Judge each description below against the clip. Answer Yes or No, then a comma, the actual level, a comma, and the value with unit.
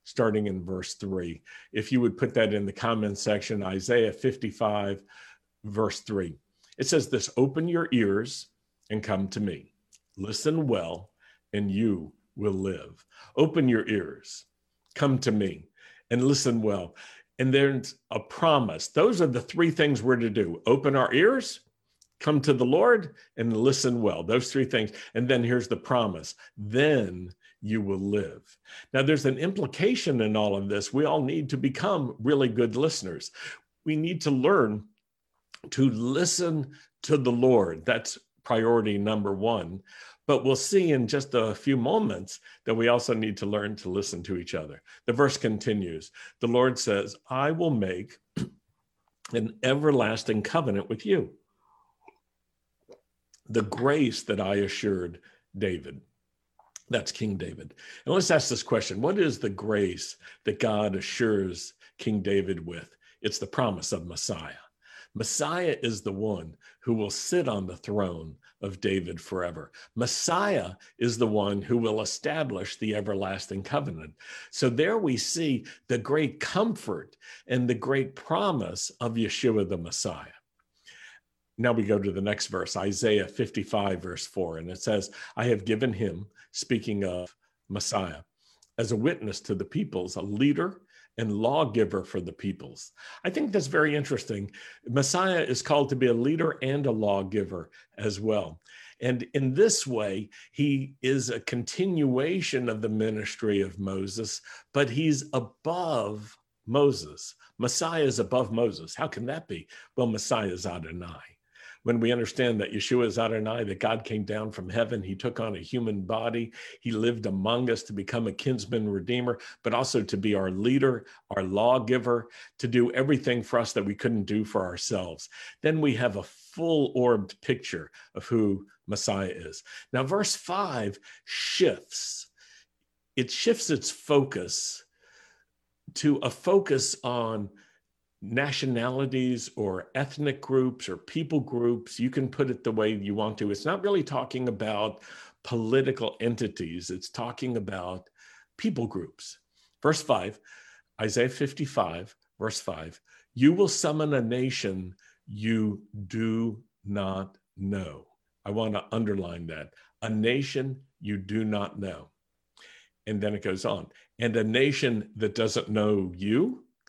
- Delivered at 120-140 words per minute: No, average, 150 wpm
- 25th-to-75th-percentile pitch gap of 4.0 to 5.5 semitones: Yes, average, 4.5 semitones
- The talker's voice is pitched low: Yes, low, 115 Hz